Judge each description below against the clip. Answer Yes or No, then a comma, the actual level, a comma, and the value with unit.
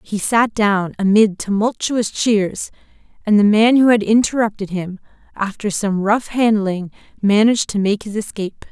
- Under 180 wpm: Yes, average, 150 wpm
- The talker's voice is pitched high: Yes, high, 210 Hz